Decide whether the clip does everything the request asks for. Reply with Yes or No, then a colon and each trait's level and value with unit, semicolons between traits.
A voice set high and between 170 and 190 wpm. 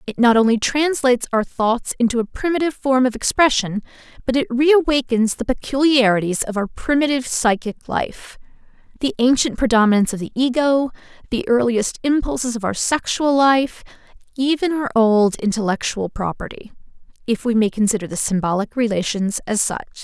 No: high, 240 Hz; average, 145 wpm